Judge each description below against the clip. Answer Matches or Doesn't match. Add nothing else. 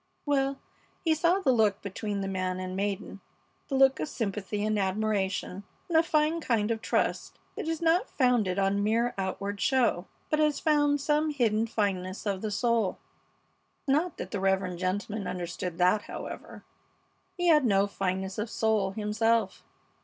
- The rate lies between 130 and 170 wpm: Matches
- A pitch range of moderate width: Doesn't match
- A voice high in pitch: Matches